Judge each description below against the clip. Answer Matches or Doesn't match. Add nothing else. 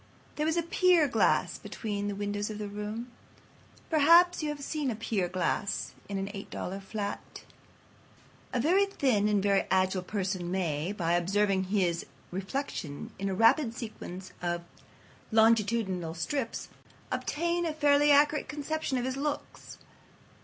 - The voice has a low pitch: Doesn't match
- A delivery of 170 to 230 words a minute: Doesn't match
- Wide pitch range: Matches